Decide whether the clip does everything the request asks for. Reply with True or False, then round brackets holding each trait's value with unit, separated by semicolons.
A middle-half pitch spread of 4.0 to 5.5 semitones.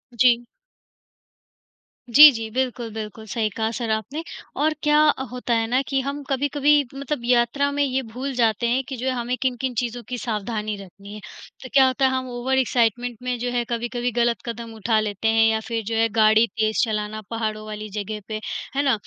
False (2.9 semitones)